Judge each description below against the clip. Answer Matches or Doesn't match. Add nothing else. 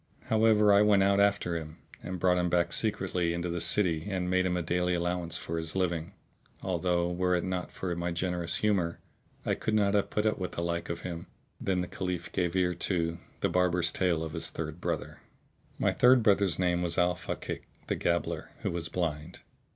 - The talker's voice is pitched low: Matches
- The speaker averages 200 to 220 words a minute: Matches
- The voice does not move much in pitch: Matches